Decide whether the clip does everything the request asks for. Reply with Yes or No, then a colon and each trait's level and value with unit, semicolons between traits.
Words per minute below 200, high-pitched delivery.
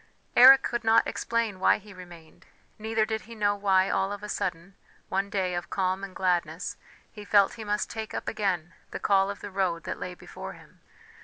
No: fast, 205 wpm; high, 195 Hz